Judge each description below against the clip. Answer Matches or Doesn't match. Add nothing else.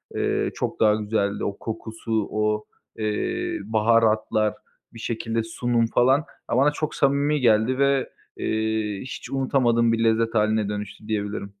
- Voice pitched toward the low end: Matches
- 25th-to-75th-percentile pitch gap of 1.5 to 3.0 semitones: Matches